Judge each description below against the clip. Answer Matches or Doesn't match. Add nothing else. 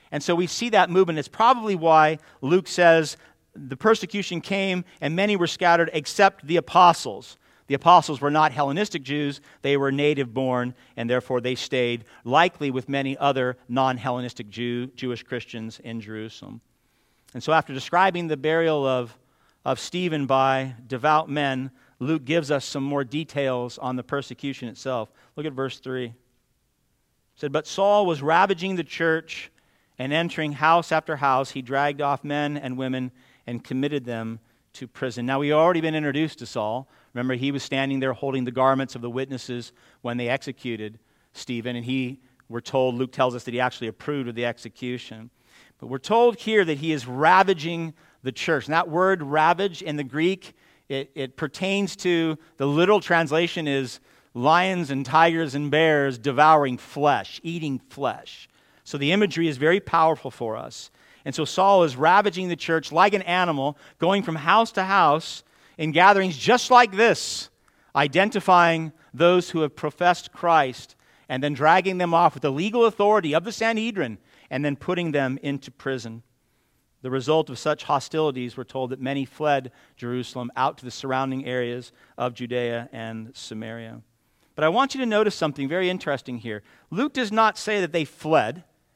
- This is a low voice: Doesn't match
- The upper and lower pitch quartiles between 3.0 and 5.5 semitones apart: Matches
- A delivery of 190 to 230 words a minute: Doesn't match